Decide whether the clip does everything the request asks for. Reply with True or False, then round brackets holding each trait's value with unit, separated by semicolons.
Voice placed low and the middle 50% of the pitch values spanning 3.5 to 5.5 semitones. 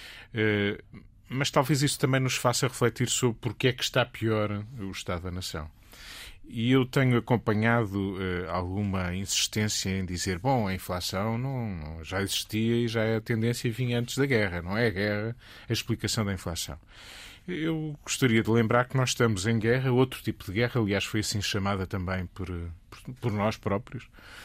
True (110 Hz; 3.9 semitones)